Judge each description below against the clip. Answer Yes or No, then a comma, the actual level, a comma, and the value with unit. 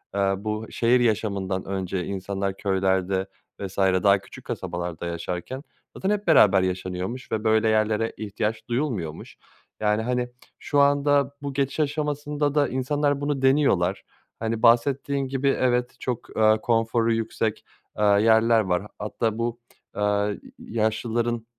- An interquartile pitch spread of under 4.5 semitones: No, average, 4.9 semitones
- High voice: No, low, 110 Hz